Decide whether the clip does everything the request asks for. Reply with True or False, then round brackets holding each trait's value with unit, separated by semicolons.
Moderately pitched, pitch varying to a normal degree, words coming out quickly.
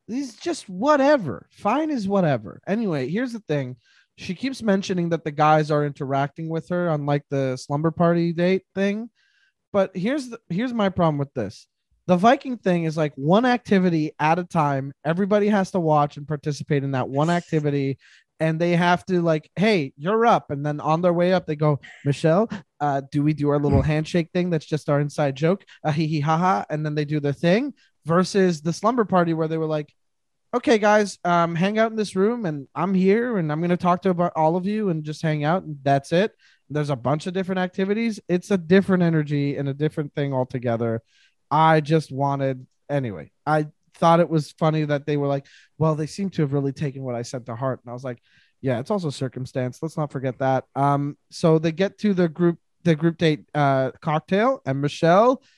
True (160 Hz; 4.6 semitones; 215 wpm)